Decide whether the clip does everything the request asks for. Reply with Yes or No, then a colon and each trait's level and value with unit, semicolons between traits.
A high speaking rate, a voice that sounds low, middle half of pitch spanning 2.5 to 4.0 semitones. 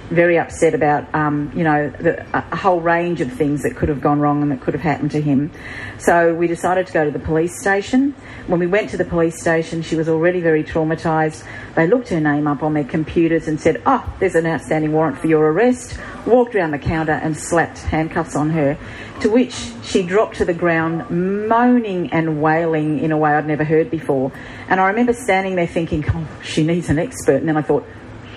No: fast, 220 wpm; medium, 160 Hz; average, 2.8 semitones